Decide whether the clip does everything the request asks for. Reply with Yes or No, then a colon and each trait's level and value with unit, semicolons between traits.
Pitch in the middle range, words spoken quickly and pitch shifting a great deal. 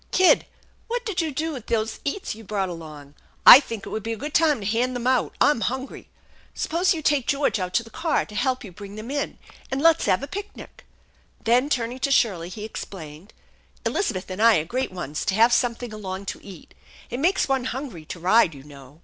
No: high, 230 Hz; fast, 230 wpm; wide, 6.6 semitones